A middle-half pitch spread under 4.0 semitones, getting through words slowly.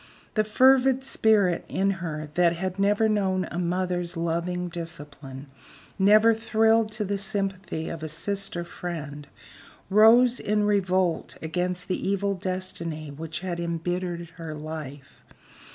Yes: average, 3.5 semitones; slow, 130 wpm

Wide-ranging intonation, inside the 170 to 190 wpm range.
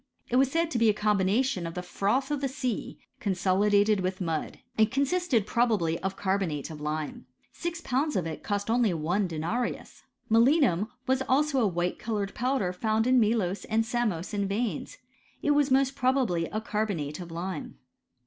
Yes: wide, 5.8 semitones; average, 180 wpm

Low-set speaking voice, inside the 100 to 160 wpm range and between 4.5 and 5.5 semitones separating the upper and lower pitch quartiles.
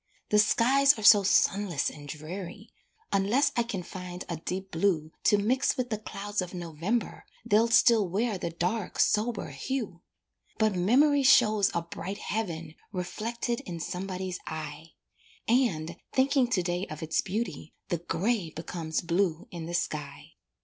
No: high, 190 Hz; average, 150 wpm; average, 4.8 semitones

